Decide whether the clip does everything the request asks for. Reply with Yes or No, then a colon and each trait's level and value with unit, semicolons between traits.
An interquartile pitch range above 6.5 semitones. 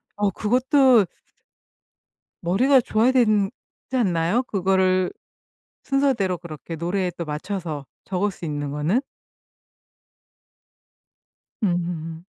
No: average, 5.1 semitones